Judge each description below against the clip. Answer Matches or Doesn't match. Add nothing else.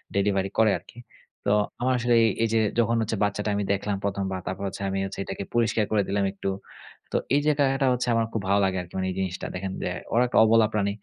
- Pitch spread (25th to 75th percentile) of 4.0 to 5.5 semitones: Doesn't match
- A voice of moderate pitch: Doesn't match